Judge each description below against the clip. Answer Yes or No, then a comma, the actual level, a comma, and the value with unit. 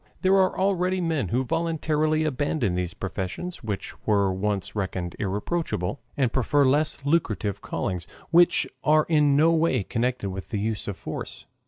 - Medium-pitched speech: No, low, 130 Hz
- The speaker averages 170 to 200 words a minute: No, average, 155 wpm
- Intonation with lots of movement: Yes, wide, 8.1 semitones